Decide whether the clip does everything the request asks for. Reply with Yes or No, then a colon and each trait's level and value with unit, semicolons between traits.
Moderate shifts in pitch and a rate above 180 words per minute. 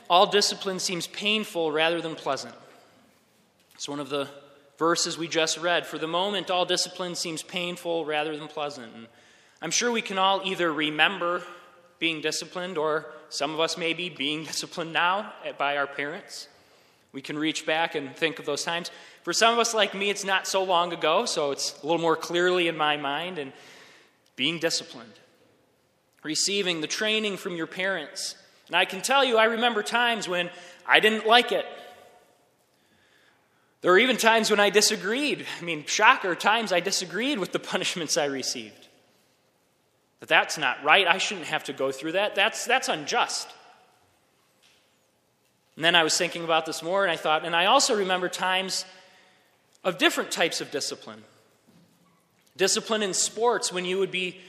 No: average, 3.7 semitones; average, 175 wpm